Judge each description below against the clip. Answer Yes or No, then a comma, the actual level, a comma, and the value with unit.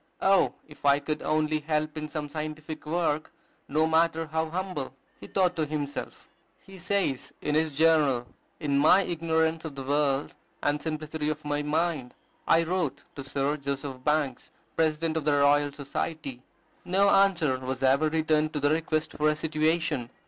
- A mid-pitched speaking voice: Yes, medium, 155 Hz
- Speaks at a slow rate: No, average, 165 wpm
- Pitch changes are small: Yes, narrow, 2.0 semitones